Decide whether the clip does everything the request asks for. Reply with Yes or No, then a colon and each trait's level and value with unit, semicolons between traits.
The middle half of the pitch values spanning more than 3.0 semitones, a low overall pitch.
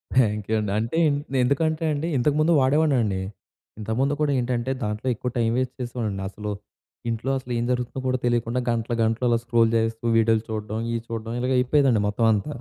No: average, 2.7 semitones; low, 120 Hz